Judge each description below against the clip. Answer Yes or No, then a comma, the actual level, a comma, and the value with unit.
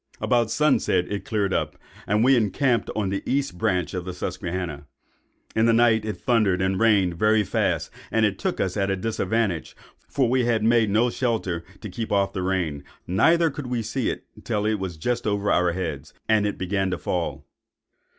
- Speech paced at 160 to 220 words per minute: Yes, average, 185 wpm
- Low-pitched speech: Yes, low, 105 Hz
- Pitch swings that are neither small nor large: Yes, average, 3.8 semitones